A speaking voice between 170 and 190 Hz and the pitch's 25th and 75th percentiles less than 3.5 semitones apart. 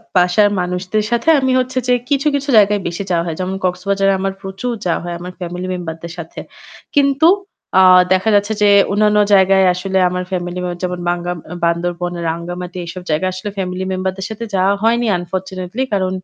Yes: medium, 185 Hz; narrow, 2.5 semitones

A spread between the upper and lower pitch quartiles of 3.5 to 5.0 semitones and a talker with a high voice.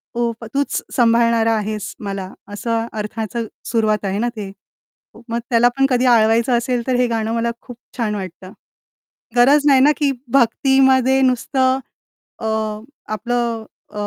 No: average, 2.7 semitones; high, 235 Hz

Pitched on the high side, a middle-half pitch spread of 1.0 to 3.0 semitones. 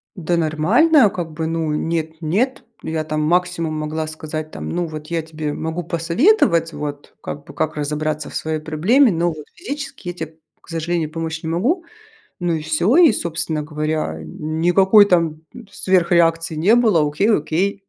No: medium, 165 Hz; narrow, 2.5 semitones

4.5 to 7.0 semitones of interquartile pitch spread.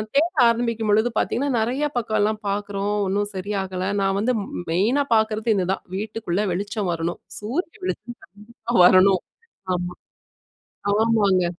No: average, 3.2 semitones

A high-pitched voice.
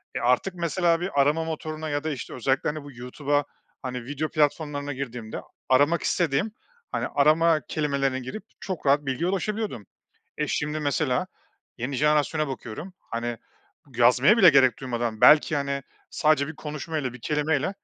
No: medium, 145 Hz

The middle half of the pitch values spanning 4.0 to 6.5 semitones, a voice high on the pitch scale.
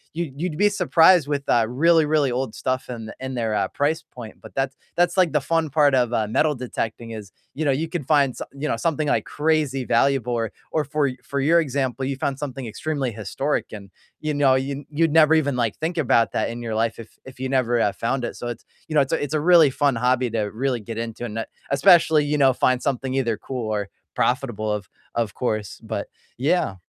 No: average, 4.3 semitones; low, 135 Hz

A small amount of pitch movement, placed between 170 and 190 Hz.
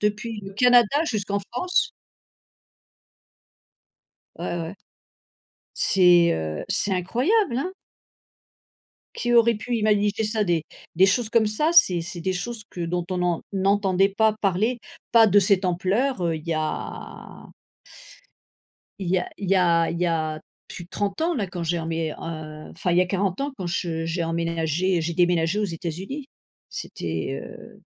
No: average, 4.2 semitones; medium, 185 Hz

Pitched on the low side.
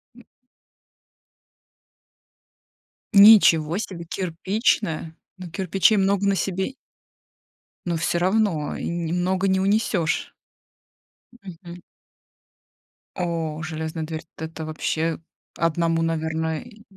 No: medium, 170 Hz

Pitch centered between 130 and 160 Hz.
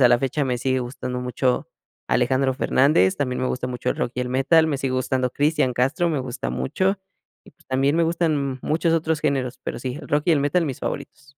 Yes: low, 135 Hz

